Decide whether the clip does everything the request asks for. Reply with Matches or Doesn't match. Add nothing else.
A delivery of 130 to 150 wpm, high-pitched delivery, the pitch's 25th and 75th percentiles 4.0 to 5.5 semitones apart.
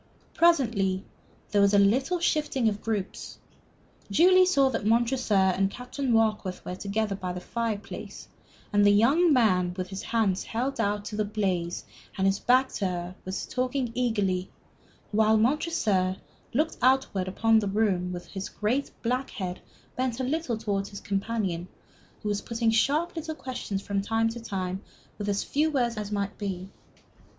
Doesn't match